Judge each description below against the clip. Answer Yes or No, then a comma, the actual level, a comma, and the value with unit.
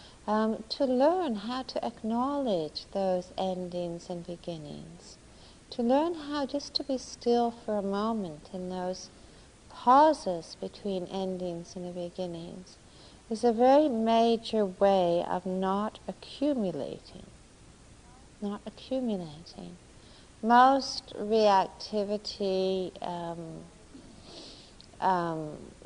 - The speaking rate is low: Yes, slow, 95 wpm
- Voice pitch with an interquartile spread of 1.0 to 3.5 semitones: No, average, 4.9 semitones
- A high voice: Yes, high, 200 Hz